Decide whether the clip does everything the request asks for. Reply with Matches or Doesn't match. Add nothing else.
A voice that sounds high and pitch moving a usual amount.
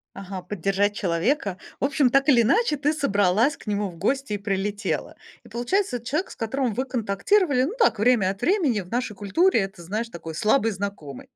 Doesn't match